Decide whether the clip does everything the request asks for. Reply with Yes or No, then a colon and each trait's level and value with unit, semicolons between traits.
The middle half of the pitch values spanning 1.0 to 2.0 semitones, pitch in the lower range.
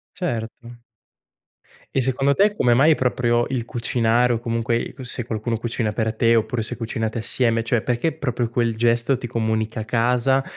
Yes: narrow, 1.7 semitones; low, 120 Hz